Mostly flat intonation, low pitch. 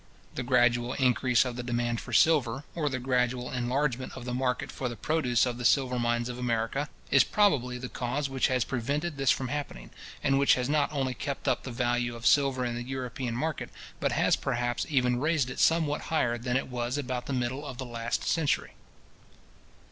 Yes: narrow, 2.2 semitones; low, 125 Hz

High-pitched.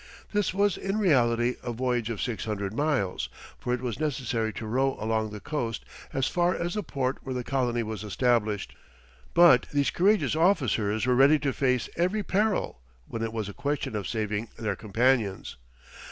No: low, 125 Hz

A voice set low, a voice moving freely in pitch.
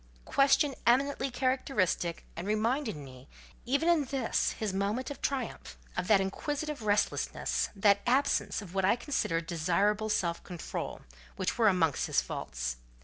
No: high, 210 Hz; wide, 6.7 semitones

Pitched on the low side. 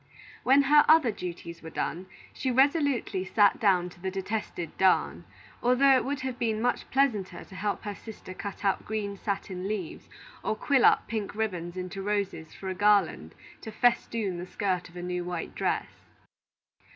No: high, 205 Hz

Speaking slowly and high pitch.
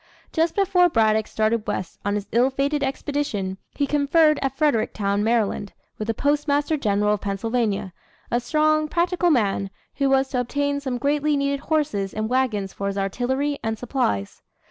No: average, 165 wpm; very high, 260 Hz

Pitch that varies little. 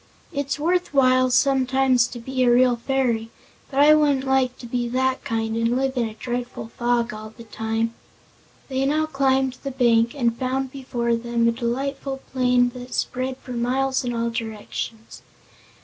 Yes: narrow, 2.2 semitones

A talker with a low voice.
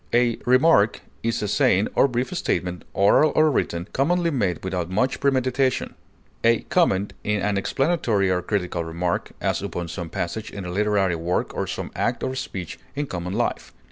Yes: low, 105 Hz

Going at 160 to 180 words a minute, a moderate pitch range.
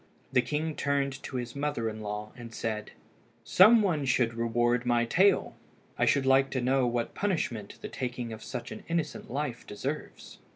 Yes: average, 175 wpm; average, 3.6 semitones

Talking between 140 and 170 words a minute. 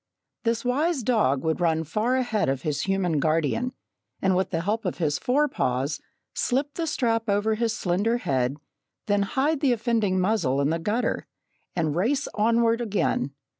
Yes: average, 165 wpm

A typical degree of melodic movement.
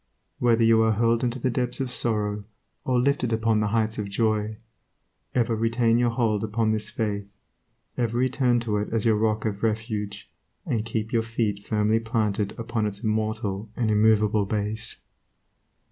No: narrow, 1.7 semitones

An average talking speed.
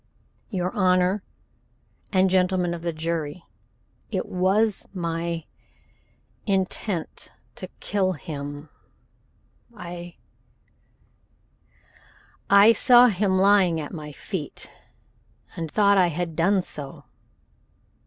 No: slow, 95 wpm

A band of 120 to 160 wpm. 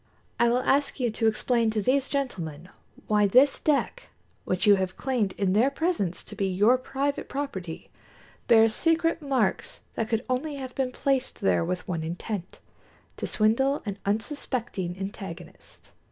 Yes: average, 155 wpm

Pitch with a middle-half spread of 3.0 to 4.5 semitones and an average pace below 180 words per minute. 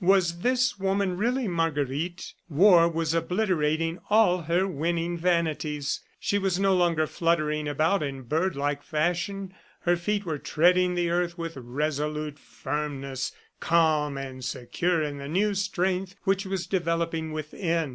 Yes: average, 3.3 semitones; average, 140 wpm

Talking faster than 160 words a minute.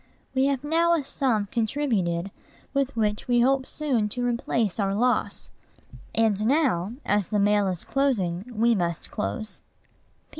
No: average, 145 wpm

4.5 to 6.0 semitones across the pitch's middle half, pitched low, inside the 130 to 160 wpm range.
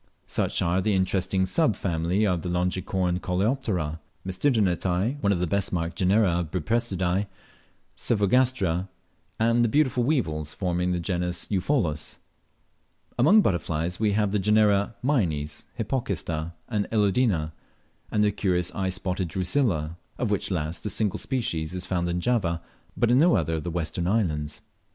No: average, 3.9 semitones; very low, 95 Hz; average, 145 wpm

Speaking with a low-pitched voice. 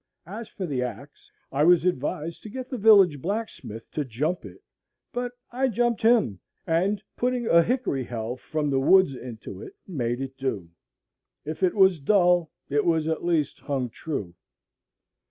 No: medium, 165 Hz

